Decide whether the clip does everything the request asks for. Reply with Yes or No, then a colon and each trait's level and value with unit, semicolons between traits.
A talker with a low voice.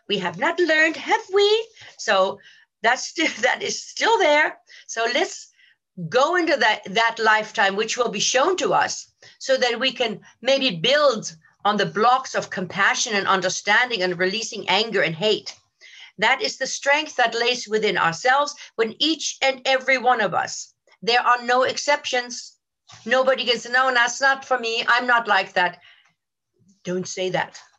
No: high, 240 Hz